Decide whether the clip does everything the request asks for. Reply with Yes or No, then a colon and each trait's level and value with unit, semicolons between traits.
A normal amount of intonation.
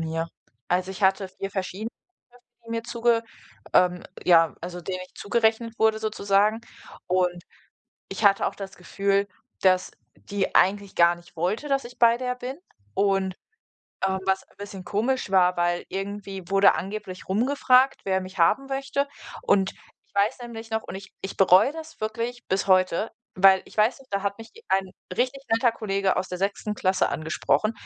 Yes: average, 3.4 semitones